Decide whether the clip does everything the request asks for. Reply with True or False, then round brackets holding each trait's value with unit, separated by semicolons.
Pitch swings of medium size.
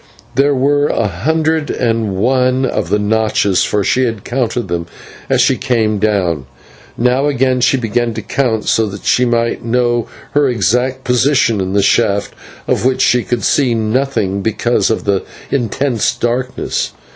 True (3.4 semitones)